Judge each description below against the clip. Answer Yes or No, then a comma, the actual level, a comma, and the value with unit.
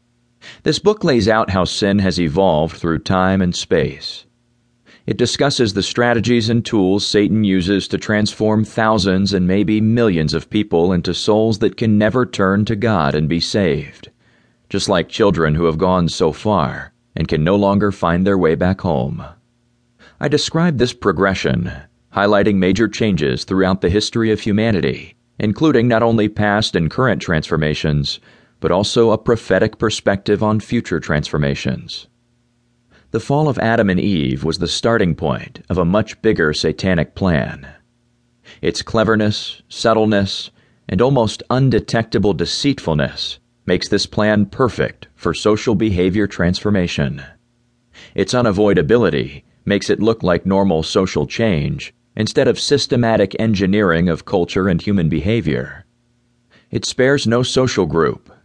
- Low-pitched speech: Yes, low, 105 Hz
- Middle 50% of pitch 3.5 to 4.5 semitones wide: Yes, average, 4.2 semitones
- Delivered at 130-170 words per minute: Yes, average, 140 wpm